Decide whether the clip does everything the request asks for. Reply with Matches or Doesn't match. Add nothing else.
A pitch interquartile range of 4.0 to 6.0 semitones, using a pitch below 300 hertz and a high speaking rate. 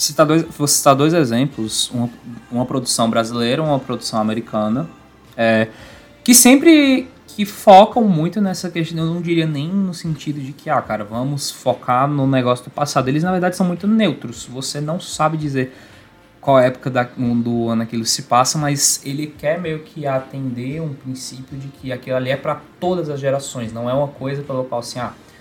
Matches